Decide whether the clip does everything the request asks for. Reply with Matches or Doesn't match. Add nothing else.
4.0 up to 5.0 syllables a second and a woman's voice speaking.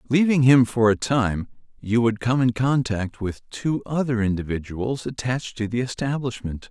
Doesn't match